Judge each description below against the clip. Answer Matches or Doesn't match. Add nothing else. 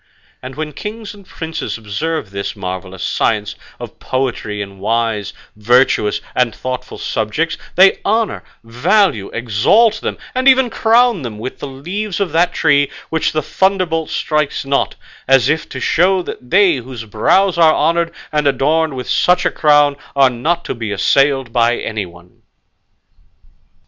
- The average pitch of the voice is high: Doesn't match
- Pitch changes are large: Matches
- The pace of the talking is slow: Doesn't match